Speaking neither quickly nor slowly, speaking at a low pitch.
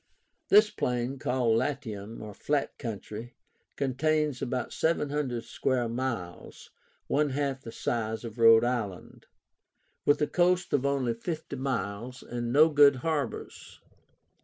No: slow, 120 wpm; low, 130 Hz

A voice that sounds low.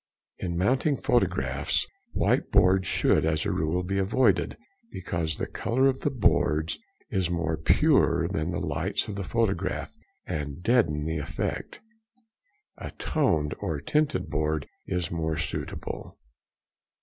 Yes: very low, 85 Hz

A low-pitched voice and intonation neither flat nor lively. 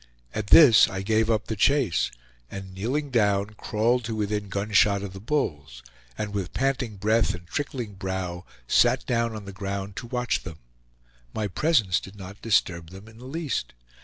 Yes: low, 105 Hz; average, 3.3 semitones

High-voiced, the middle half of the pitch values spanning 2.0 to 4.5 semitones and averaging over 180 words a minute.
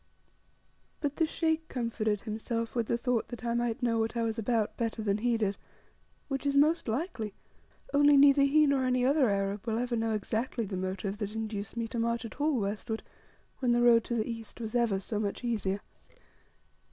Yes: high, 230 Hz; average, 2.7 semitones; average, 200 wpm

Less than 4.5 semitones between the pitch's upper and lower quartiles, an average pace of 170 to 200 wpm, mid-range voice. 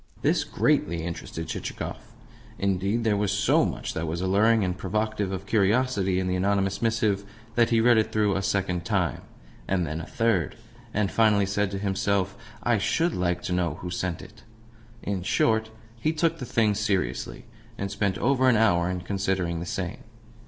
No: average, 3.1 semitones; average, 180 wpm; low, 100 Hz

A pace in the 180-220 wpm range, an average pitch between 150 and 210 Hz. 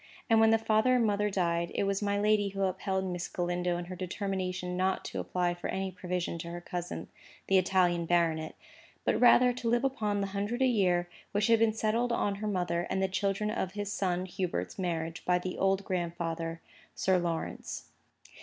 Yes: average, 195 wpm; high, 190 Hz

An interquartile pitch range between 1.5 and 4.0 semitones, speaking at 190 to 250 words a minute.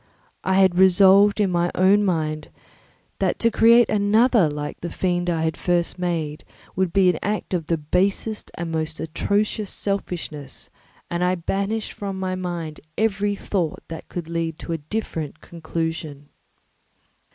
No: average, 3.6 semitones; average, 150 wpm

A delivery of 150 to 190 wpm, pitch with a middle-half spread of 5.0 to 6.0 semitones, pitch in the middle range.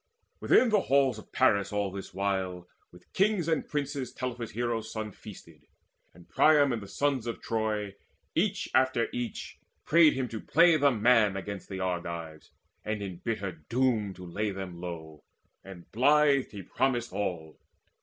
No: average, 160 wpm; wide, 5.6 semitones; low, 110 Hz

